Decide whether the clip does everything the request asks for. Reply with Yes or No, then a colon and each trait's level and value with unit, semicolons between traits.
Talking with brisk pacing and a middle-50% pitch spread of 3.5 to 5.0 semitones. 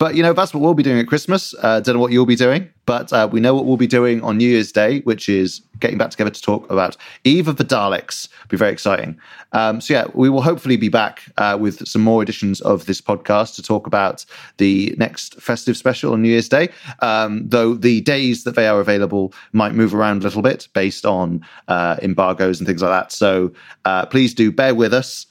Yes: fast, 240 wpm; average, 4.0 semitones